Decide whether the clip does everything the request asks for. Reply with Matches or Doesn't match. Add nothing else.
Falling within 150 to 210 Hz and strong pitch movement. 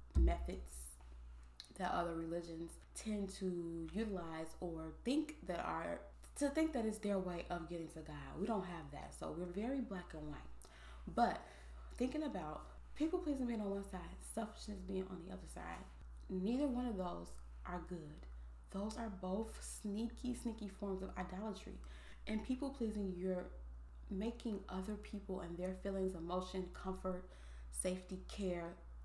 Matches